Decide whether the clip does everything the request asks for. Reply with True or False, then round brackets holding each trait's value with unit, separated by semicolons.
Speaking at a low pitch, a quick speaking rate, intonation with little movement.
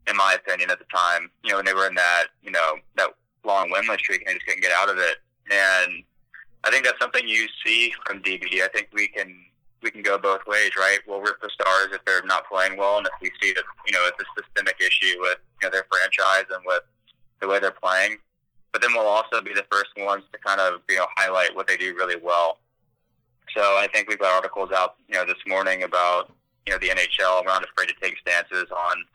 True (95 Hz; 245 wpm; 1.4 semitones)